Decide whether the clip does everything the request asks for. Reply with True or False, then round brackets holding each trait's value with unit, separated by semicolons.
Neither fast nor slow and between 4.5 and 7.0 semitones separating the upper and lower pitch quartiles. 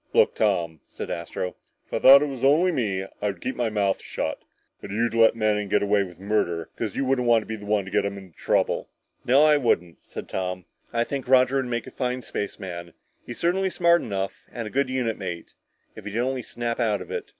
False (230 wpm; 4.8 semitones)